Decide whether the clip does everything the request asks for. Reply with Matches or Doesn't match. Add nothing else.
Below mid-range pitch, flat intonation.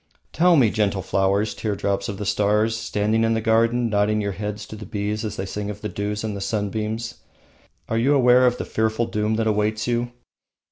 Matches